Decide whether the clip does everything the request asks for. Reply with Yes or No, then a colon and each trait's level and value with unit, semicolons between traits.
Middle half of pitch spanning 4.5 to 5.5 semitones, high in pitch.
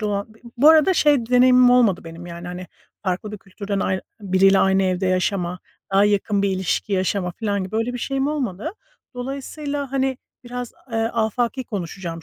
Yes: average, 4.8 semitones; high, 205 Hz